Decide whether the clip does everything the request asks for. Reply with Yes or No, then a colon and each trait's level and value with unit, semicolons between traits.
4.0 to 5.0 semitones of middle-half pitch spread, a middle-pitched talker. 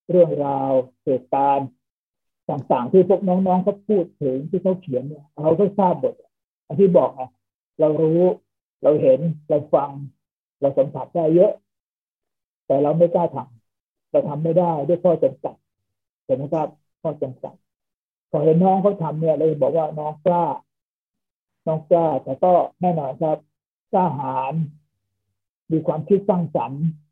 Yes: average, 4.6 semitones; medium, 155 Hz